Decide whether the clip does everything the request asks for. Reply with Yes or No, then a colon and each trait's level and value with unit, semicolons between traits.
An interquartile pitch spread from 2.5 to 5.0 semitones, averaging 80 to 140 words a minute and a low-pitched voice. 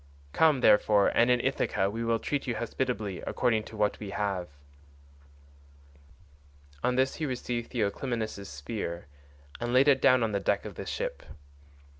No: average, 3.7 semitones; average, 155 wpm; low, 115 Hz